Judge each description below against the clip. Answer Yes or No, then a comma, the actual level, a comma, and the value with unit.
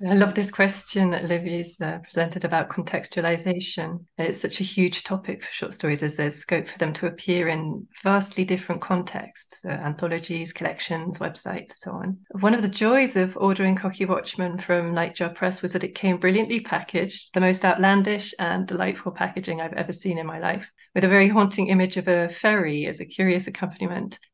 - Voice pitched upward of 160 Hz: Yes, medium, 185 Hz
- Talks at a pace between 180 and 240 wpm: Yes, average, 185 wpm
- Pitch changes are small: Yes, narrow, 2.2 semitones